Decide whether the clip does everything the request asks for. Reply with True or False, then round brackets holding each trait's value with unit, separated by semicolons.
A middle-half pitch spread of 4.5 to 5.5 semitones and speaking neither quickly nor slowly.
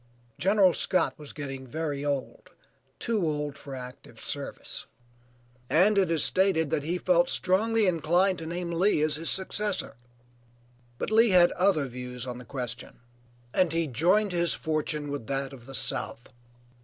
True (4.9 semitones; 155 wpm)